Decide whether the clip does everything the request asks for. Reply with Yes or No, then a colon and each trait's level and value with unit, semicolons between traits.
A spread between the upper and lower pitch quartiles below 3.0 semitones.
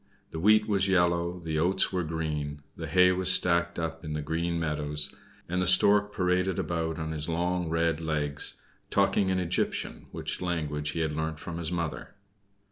Yes: narrow, 2.5 semitones